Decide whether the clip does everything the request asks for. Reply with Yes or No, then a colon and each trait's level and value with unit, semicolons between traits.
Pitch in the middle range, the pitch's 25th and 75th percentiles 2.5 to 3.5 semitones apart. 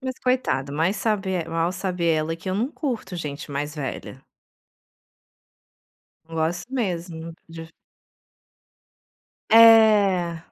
No: medium, 175 Hz; average, 4.7 semitones